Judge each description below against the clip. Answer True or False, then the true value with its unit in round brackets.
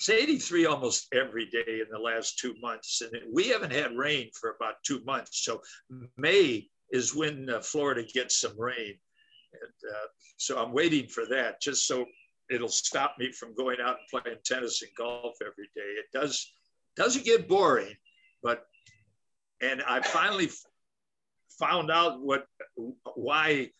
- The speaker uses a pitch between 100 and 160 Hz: True (140 Hz)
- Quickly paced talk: False (155 wpm)